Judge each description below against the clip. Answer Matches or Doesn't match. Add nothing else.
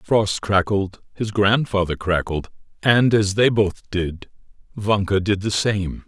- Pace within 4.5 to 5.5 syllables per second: Doesn't match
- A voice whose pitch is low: Matches